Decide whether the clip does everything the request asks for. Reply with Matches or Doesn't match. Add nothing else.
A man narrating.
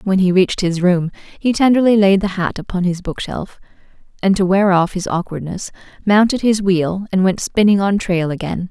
Doesn't match